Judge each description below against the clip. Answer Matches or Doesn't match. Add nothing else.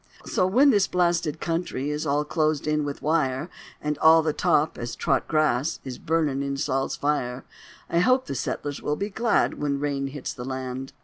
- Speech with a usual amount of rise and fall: Matches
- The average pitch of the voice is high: Doesn't match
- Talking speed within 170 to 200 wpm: Matches